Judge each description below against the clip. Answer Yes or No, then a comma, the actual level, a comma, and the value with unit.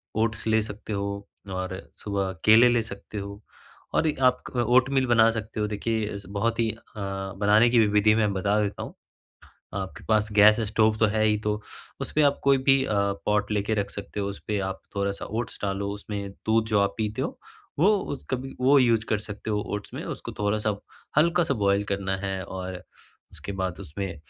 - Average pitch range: No, narrow, 2.2 semitones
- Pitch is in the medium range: No, low, 105 Hz